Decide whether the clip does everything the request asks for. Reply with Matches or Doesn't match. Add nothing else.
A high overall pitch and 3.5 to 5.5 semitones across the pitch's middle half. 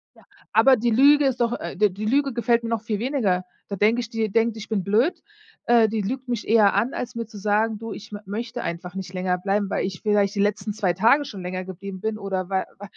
Doesn't match